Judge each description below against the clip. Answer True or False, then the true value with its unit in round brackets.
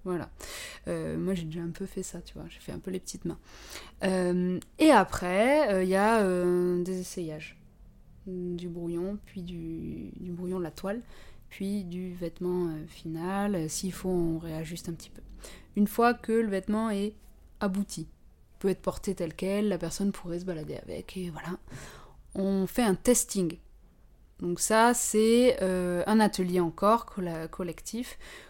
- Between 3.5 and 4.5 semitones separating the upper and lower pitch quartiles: False (2.7 semitones)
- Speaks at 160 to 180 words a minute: True (170 wpm)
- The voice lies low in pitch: False (185 Hz)